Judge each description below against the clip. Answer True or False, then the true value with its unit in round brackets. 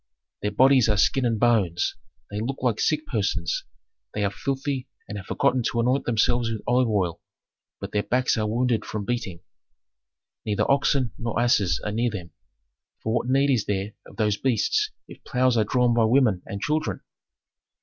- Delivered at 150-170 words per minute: False (180 wpm)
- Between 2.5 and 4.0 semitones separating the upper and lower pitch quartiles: True (3.6 semitones)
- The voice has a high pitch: False (115 Hz)